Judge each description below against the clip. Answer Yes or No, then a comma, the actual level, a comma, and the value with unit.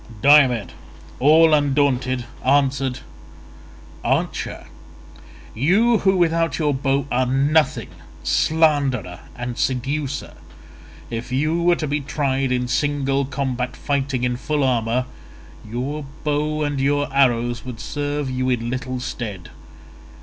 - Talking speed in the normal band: No, slow, 115 wpm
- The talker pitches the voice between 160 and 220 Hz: No, low, 135 Hz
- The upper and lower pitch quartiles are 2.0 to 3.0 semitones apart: Yes, average, 2.7 semitones